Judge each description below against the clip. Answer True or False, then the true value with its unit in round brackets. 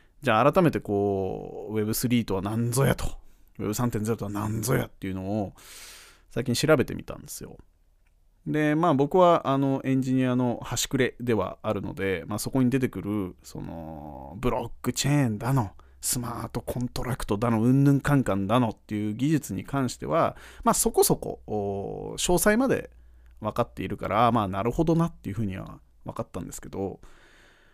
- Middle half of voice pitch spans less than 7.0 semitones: True (5.5 semitones)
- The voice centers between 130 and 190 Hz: False (115 Hz)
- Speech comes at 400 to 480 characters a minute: False (345 characters per minute)